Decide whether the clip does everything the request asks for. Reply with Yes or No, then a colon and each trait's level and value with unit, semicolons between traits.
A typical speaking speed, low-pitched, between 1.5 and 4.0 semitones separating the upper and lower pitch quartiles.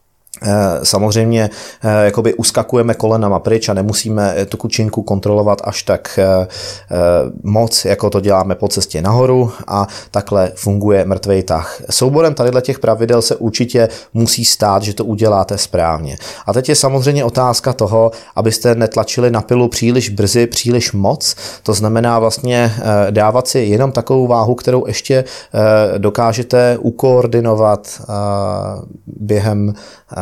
Yes: average, 125 wpm; low, 110 Hz; average, 2.8 semitones